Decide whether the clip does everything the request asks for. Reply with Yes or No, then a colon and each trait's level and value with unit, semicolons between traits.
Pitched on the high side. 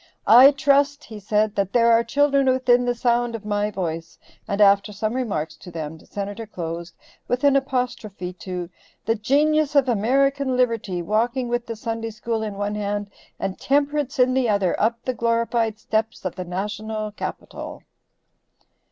Yes: high, 225 Hz